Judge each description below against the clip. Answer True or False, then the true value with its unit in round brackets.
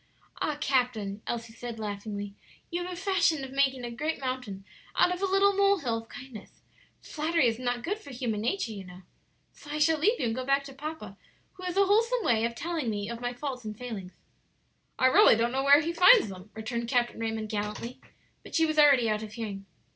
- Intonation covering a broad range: True (6.1 semitones)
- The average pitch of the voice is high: True (250 Hz)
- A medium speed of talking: False (220 wpm)